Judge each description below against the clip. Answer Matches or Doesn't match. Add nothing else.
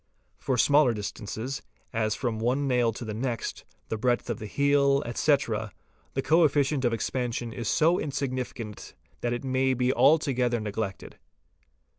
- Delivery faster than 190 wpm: Doesn't match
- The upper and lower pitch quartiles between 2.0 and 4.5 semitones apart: Matches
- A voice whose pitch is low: Matches